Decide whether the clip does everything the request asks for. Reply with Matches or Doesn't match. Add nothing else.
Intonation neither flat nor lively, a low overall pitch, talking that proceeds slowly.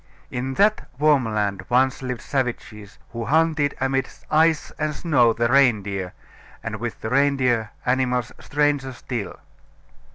Matches